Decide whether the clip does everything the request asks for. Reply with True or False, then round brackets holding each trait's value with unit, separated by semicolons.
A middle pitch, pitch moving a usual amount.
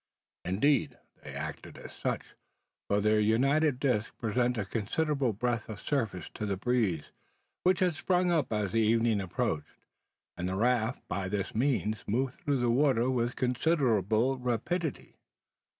False (120 Hz; 4.2 semitones)